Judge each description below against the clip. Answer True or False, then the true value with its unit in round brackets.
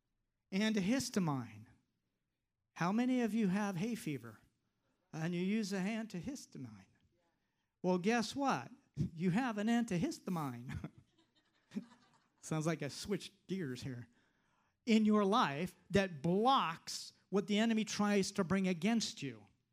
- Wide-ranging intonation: True (7.4 semitones)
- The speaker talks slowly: True (120 wpm)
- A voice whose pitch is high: True (195 Hz)